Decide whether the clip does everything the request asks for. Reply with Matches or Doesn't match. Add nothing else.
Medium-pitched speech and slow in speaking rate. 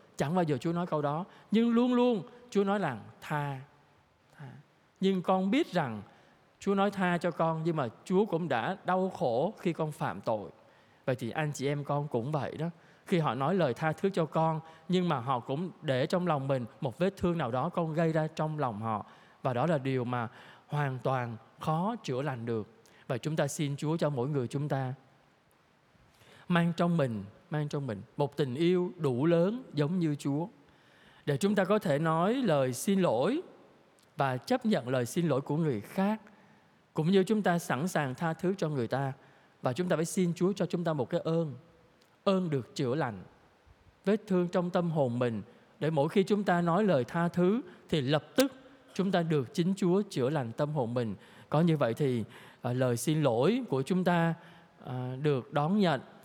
Doesn't match